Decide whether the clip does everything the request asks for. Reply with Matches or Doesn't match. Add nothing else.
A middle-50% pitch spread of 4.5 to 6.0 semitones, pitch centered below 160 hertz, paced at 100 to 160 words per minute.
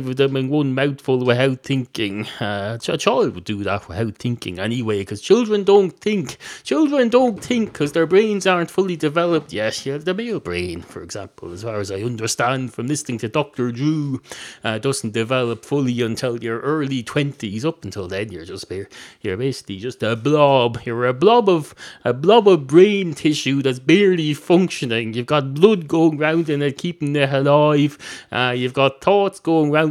Doesn't match